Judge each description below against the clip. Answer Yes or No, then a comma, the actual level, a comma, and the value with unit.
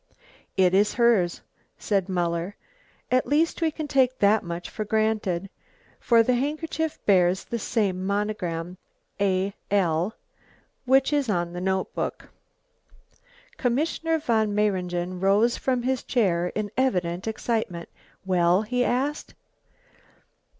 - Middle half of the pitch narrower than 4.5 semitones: No, average, 5.3 semitones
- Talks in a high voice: Yes, high, 205 Hz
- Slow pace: Yes, slow, 120 wpm